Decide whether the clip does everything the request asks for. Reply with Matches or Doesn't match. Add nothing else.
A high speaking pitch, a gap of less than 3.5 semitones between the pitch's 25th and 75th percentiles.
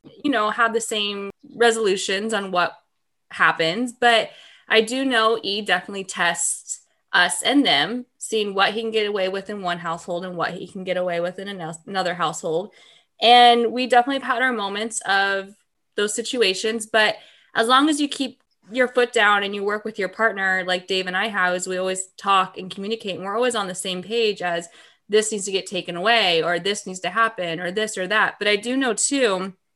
Doesn't match